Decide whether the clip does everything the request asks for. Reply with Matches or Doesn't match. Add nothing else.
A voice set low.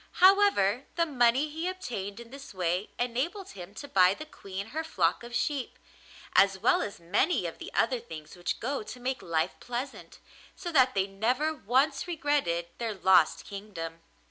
Doesn't match